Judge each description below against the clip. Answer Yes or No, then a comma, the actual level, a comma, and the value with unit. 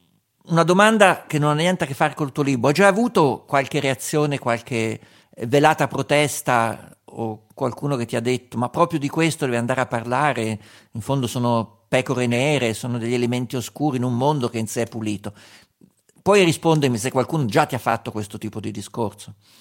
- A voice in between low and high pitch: No, low, 125 Hz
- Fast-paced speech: Yes, fast, 195 wpm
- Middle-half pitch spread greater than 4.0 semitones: Yes, average, 4.6 semitones